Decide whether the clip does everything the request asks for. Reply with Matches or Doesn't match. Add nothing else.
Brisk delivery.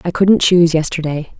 Doesn't match